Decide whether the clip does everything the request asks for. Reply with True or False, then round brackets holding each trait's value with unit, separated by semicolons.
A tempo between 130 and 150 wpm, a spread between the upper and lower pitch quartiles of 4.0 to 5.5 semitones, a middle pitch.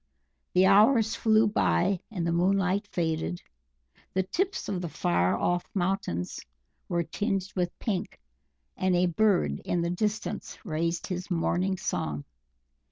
False (135 wpm; 3.0 semitones; 180 Hz)